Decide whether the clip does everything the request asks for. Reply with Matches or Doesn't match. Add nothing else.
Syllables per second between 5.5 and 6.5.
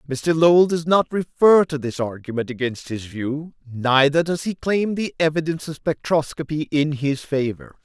Doesn't match